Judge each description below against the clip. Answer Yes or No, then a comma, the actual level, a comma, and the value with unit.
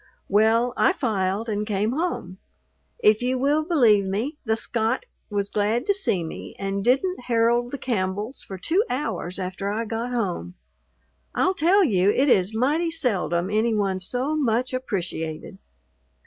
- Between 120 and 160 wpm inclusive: Yes, average, 155 wpm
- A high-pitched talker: Yes, high, 225 Hz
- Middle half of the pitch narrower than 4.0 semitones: No, average, 4.8 semitones